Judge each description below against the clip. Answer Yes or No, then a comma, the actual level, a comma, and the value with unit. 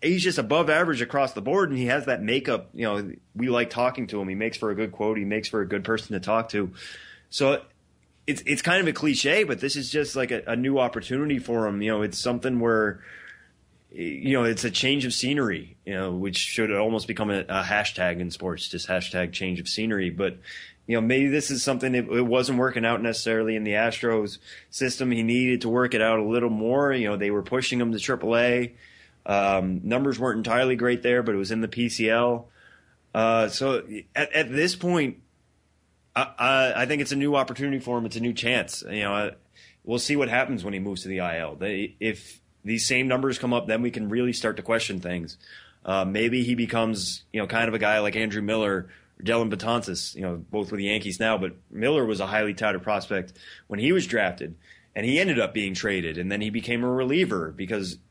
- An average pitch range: Yes, average, 3.5 semitones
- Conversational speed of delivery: No, fast, 225 wpm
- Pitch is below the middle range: Yes, low, 115 Hz